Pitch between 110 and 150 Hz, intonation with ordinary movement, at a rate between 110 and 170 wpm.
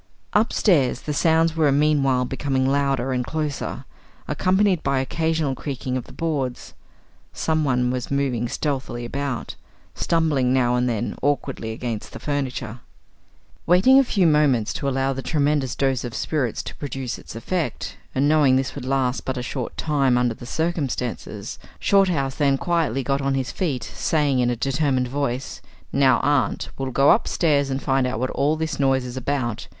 Yes: low, 135 Hz; average, 3.0 semitones; average, 165 wpm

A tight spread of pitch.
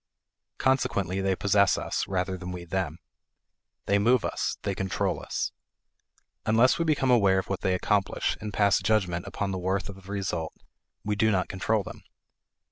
Yes: narrow, 1.9 semitones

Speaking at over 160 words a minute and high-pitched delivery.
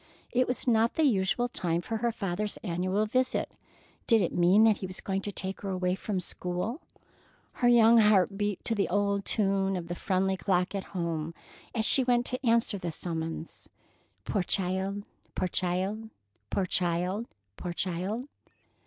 Yes: average, 170 wpm; high, 195 Hz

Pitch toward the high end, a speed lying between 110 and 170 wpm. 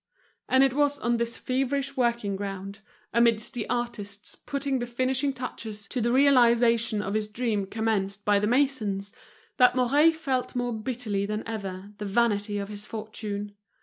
Yes: high, 230 Hz; average, 160 wpm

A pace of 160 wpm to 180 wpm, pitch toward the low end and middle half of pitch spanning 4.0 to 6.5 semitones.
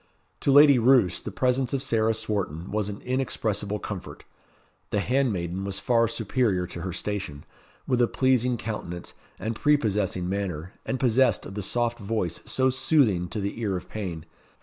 Yes: average, 165 wpm; low, 110 Hz; average, 4.8 semitones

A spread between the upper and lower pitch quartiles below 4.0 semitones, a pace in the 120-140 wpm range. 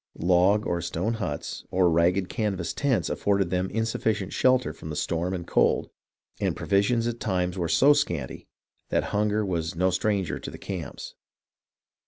No: average, 3.5 semitones; average, 160 wpm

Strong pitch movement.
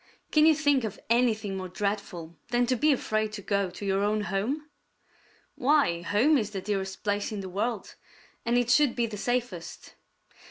No: average, 3.9 semitones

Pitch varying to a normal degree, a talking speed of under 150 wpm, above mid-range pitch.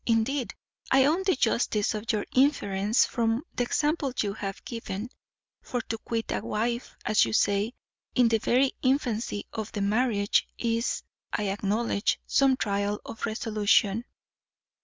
Yes: average, 3.2 semitones; average, 140 wpm; high, 225 Hz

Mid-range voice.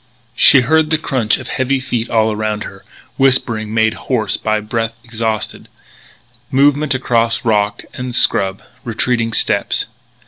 No: low, 115 Hz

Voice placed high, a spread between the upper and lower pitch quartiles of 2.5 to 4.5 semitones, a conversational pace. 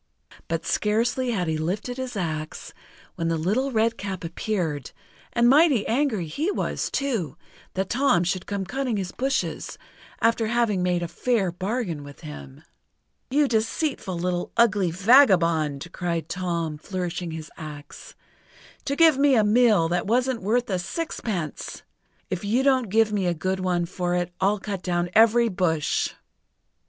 No: high, 195 Hz; wide, 5.5 semitones; average, 150 wpm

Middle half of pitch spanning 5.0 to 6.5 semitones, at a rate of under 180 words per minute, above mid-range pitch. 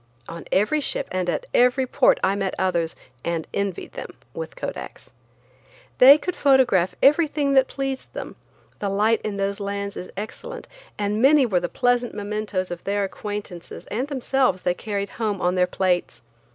Yes: wide, 5.6 semitones; average, 160 wpm; high, 205 Hz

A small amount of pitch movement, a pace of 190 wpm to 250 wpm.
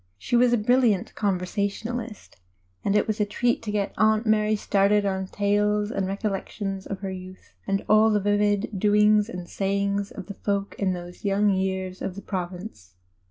No: narrow, 1.6 semitones; average, 175 wpm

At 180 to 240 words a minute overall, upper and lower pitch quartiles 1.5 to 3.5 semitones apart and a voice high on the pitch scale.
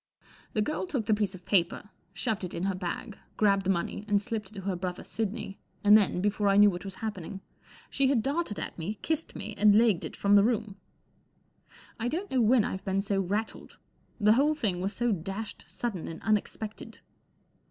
Yes: average, 200 wpm; narrow, 2.6 semitones; high, 205 Hz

